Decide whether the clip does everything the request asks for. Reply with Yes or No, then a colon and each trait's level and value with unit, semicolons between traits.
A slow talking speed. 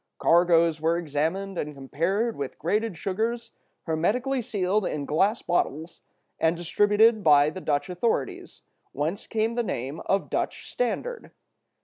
Yes: slow, 130 wpm